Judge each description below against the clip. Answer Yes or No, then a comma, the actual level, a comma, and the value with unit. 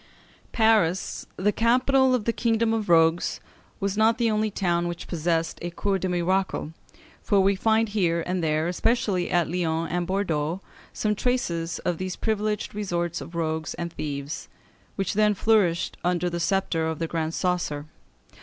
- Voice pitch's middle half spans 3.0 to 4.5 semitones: Yes, average, 4.1 semitones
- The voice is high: No, medium, 180 Hz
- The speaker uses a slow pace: No, average, 165 wpm